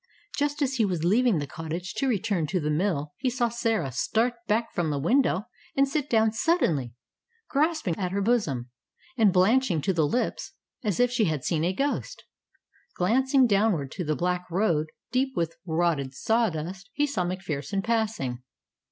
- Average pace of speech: Yes, average, 170 wpm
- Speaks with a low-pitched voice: No, high, 195 Hz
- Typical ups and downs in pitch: No, wide, 6.8 semitones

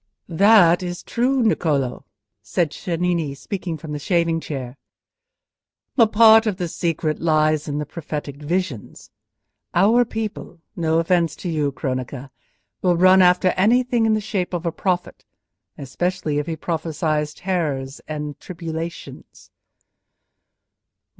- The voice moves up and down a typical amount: Yes, average, 3.7 semitones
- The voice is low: No, medium, 170 Hz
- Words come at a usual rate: No, slow, 120 wpm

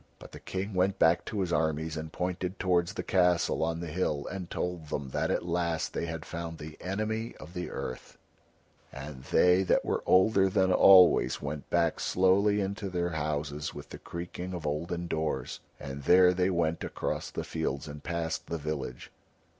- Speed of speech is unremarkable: Yes, average, 185 wpm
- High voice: No, very low, 85 Hz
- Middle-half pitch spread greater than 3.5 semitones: No, average, 2.9 semitones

